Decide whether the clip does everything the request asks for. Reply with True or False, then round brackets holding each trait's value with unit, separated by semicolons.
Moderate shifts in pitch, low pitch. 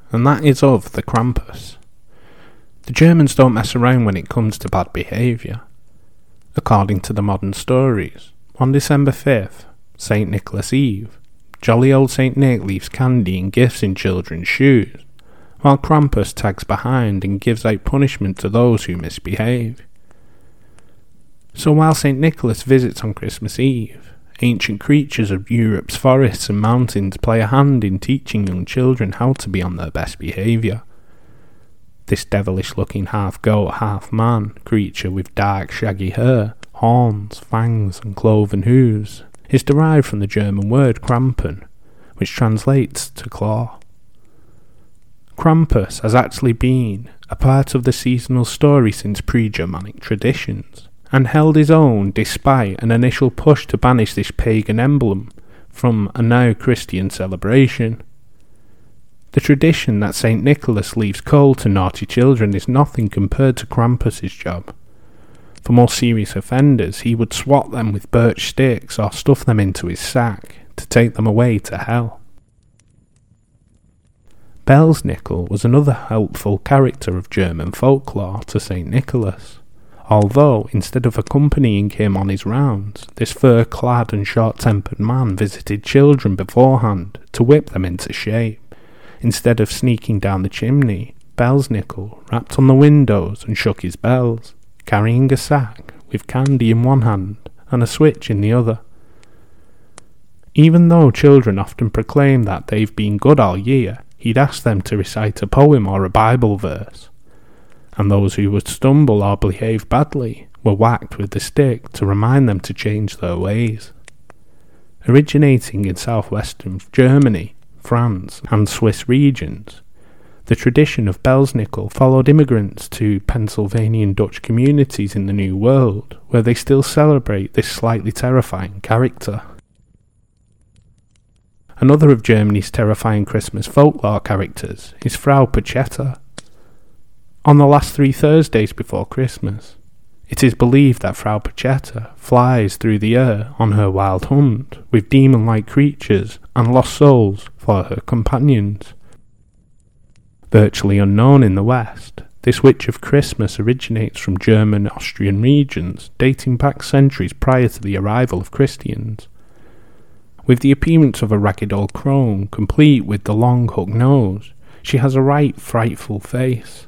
True (4.3 semitones; 115 Hz)